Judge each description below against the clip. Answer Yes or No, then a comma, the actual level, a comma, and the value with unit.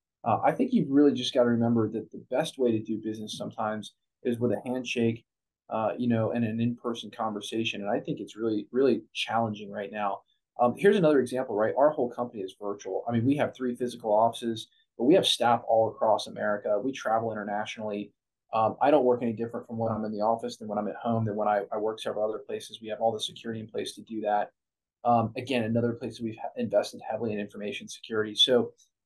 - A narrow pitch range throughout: Yes, narrow, 2.2 semitones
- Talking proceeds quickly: Yes, fast, 230 wpm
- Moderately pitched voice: No, low, 115 Hz